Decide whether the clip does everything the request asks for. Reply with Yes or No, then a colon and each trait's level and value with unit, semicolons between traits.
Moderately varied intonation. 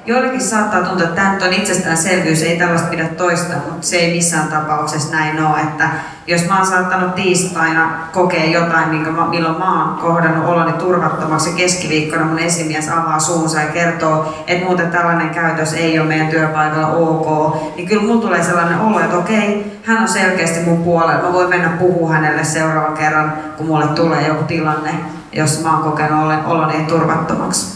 No: narrow, 2.1 semitones